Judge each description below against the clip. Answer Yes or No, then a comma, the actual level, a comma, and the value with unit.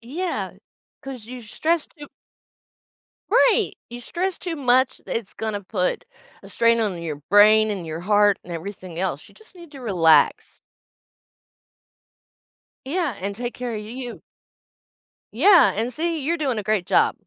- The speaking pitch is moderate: No, high, 230 Hz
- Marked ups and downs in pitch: Yes, wide, 6.2 semitones